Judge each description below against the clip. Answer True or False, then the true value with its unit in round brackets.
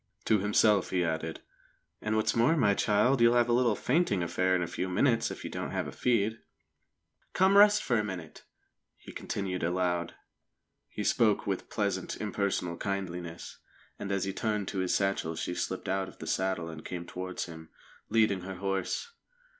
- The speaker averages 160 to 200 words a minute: True (185 wpm)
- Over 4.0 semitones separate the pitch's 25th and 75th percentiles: False (3.4 semitones)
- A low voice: True (100 Hz)